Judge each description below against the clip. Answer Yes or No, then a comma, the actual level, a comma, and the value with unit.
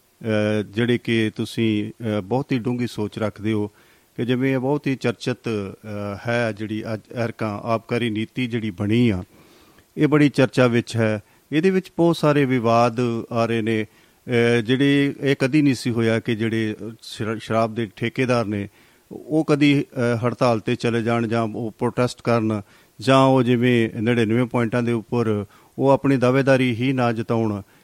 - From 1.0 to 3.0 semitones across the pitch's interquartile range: Yes, narrow, 2.4 semitones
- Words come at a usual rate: Yes, average, 150 wpm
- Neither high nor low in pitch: No, low, 120 Hz